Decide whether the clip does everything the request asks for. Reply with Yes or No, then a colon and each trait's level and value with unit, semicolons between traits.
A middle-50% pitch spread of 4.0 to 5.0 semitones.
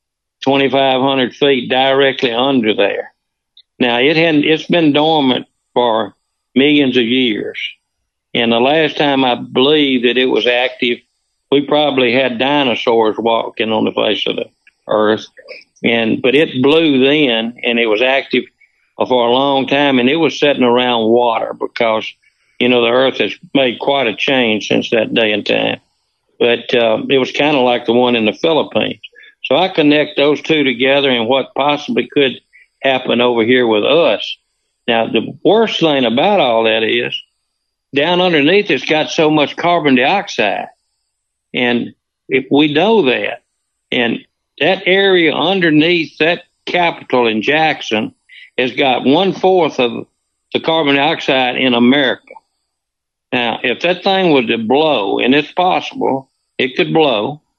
Yes: average, 4.4 semitones